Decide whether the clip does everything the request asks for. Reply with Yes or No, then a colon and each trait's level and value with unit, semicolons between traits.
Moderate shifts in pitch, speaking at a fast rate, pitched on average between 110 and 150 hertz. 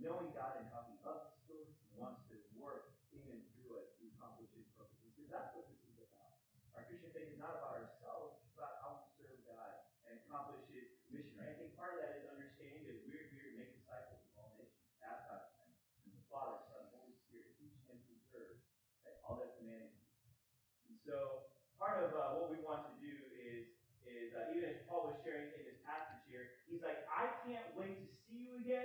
No: wide, 5.9 semitones; fast, 210 wpm; low, 135 Hz